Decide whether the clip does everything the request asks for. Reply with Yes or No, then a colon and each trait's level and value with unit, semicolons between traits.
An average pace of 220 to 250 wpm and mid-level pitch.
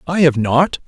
No: fast, 205 wpm; medium, 150 Hz